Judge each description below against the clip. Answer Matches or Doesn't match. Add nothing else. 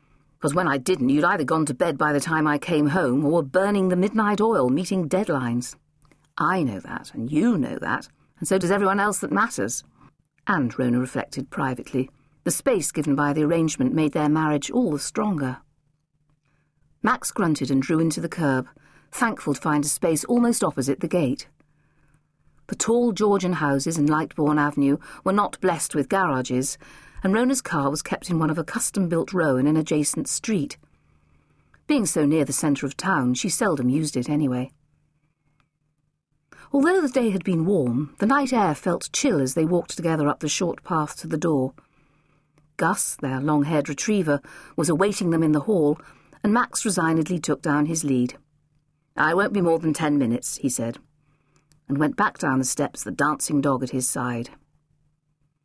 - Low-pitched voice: Doesn't match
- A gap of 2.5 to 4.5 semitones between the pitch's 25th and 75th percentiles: Matches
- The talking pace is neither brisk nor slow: Matches